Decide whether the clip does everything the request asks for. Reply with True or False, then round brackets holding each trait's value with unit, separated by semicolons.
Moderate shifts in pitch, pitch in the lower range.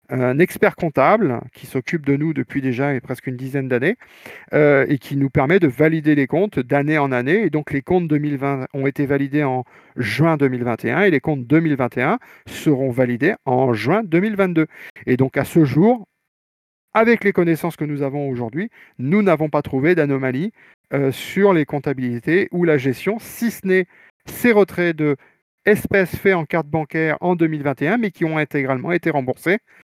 False (4.5 semitones; 150 Hz)